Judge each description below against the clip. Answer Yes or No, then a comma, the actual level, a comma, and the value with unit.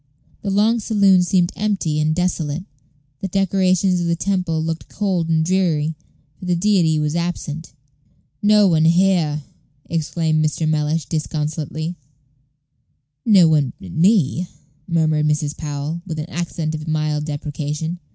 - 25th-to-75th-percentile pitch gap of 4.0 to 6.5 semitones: No, average, 3.1 semitones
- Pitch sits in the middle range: Yes, medium, 165 Hz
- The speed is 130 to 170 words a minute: Yes, slow, 135 wpm